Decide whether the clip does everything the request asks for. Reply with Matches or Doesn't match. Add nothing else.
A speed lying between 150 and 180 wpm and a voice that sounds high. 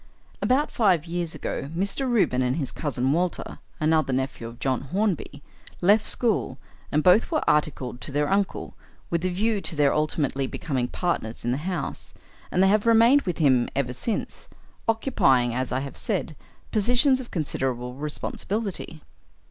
Doesn't match